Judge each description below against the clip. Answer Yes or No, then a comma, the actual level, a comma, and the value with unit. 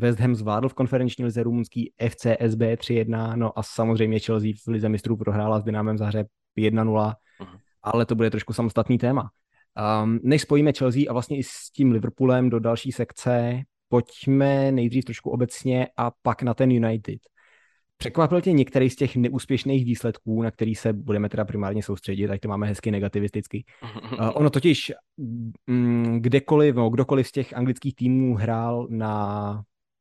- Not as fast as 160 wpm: No, average, 165 wpm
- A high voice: No, low, 115 Hz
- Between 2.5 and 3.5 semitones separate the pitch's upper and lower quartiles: Yes, average, 2.9 semitones